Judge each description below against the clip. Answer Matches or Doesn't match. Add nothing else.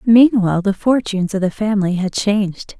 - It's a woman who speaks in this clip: Matches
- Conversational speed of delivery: Matches